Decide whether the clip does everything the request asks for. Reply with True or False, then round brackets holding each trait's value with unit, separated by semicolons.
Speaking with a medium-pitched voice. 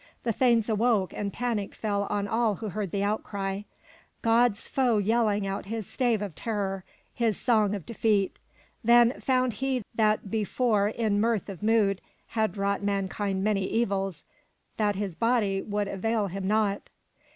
False (210 Hz)